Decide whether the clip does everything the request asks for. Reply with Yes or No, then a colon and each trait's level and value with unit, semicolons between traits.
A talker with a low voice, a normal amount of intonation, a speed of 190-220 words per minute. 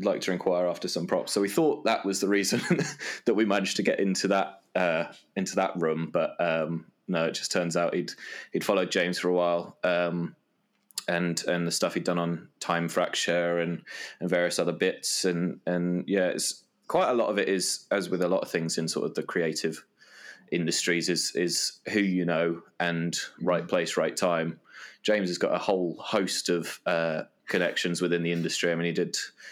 No: very low, 85 Hz; narrow, 1.3 semitones; fast, 205 wpm